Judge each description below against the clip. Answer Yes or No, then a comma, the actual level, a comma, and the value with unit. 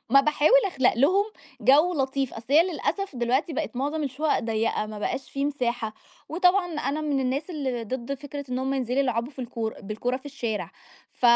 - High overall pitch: Yes, very high, 270 Hz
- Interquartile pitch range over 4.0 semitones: No, average, 3.7 semitones